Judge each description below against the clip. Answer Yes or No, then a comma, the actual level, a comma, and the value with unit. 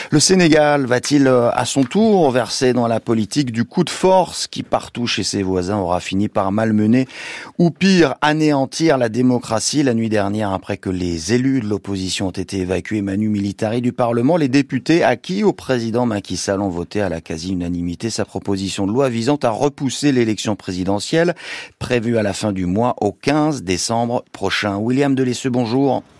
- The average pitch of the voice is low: Yes, low, 115 Hz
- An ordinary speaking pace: Yes, average, 175 wpm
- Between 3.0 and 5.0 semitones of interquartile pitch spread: No, wide, 5.4 semitones